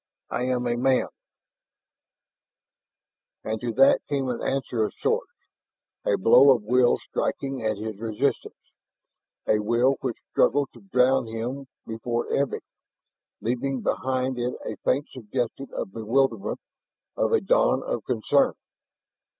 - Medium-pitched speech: No, low, 125 Hz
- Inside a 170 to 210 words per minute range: No, slow, 135 wpm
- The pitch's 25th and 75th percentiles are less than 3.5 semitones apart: Yes, average, 3.0 semitones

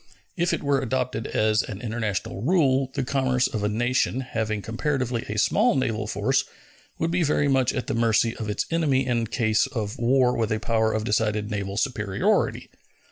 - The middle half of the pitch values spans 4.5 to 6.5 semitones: No, average, 3.5 semitones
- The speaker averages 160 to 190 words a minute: Yes, average, 185 wpm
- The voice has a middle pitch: No, low, 120 Hz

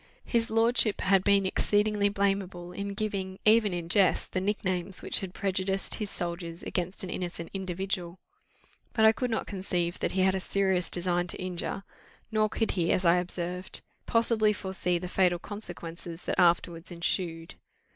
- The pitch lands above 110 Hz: Yes, high, 190 Hz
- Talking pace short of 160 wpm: No, average, 165 wpm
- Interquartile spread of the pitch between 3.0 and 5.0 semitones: No, narrow, 2.4 semitones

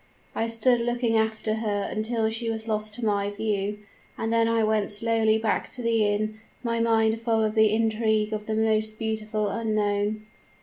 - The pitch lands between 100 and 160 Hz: No, high, 220 Hz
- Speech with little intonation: Yes, narrow, 1.1 semitones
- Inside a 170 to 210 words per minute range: Yes, average, 175 wpm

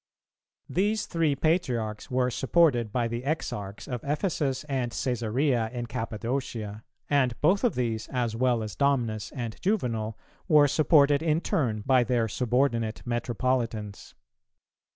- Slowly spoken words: Yes, slow, 130 wpm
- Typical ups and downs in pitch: Yes, average, 4.0 semitones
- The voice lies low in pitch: Yes, low, 125 Hz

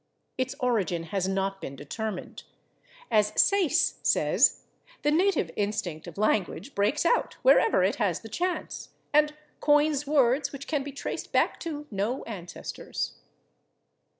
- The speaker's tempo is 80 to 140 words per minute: Yes, slow, 135 wpm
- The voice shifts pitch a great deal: Yes, wide, 7.2 semitones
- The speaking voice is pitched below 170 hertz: No, high, 235 Hz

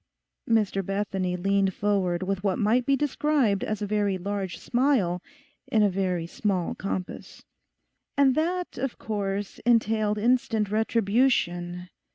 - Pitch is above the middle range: Yes, high, 205 Hz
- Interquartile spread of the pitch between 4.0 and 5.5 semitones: No, average, 3.3 semitones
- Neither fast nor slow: No, slow, 130 wpm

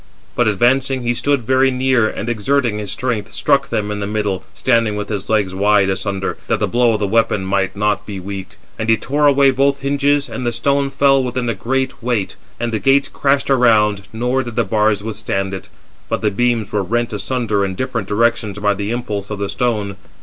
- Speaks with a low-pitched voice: Yes, low, 115 Hz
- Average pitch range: Yes, average, 3.8 semitones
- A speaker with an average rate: No, fast, 215 wpm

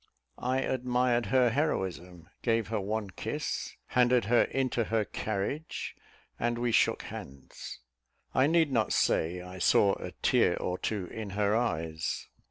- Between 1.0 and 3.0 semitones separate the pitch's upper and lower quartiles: No, average, 4.6 semitones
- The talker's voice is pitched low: Yes, low, 110 Hz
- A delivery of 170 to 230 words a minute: No, average, 145 wpm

